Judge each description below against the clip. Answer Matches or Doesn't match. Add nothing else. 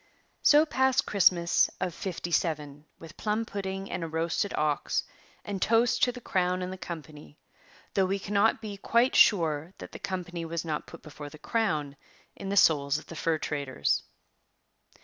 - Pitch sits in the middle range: Matches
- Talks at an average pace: Matches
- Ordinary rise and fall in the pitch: Matches